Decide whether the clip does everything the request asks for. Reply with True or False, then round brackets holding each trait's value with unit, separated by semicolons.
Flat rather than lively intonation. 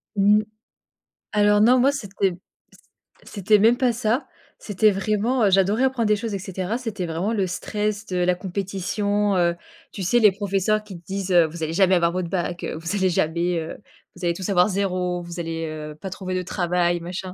False (3.0 semitones)